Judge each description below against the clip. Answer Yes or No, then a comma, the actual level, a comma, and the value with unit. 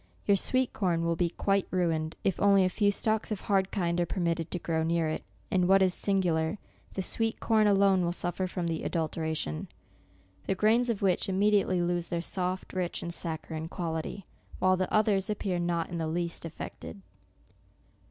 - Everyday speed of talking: Yes, average, 185 wpm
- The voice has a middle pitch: Yes, medium, 180 Hz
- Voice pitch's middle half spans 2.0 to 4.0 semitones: Yes, average, 2.8 semitones